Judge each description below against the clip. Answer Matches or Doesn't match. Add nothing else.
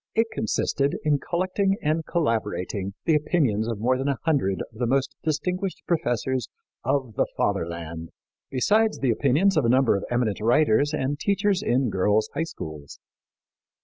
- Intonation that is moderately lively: Doesn't match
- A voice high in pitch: Doesn't match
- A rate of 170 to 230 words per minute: Doesn't match